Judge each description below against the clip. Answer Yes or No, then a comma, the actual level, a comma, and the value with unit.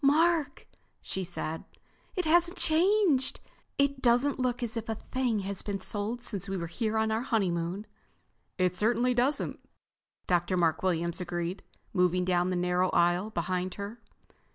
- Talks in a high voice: Yes, high, 205 Hz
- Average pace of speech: Yes, average, 155 wpm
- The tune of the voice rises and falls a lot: Yes, wide, 5.8 semitones